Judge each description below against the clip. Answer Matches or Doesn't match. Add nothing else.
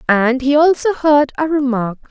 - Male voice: Doesn't match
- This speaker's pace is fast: Doesn't match